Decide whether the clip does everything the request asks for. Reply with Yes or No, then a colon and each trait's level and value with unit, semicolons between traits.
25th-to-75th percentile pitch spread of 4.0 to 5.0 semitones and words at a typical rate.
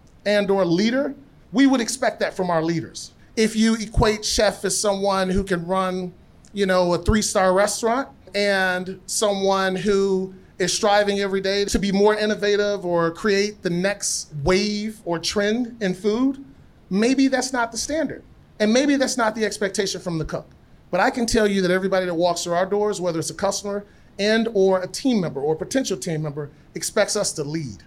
No: narrow, 2.6 semitones; average, 185 wpm